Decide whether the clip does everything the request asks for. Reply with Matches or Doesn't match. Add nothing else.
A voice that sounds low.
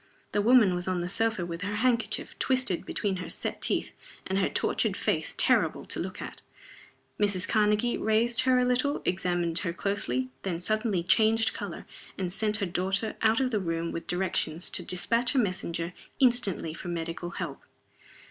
Doesn't match